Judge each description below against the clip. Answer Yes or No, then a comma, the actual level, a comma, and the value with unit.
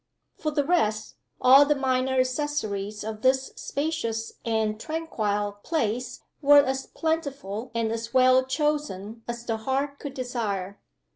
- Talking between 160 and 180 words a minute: No, slow, 135 wpm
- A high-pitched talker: Yes, very high, 255 Hz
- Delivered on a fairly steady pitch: No, average, 4.5 semitones